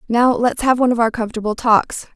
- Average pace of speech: No, fast, 225 wpm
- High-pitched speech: Yes, high, 235 Hz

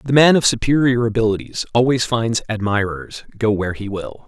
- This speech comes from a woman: No, male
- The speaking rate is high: No, average, 170 wpm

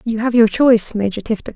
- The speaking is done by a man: No, female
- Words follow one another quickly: Yes, fast, 230 wpm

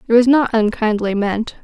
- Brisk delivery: No, average, 185 wpm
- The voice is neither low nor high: No, high, 225 Hz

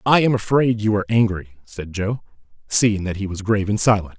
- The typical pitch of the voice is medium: No, low, 105 Hz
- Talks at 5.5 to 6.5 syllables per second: Yes, 5.9 syllables/s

